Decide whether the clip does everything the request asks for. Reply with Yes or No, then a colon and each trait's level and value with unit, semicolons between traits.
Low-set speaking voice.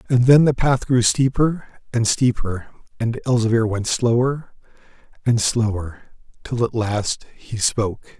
Yes: low, 115 Hz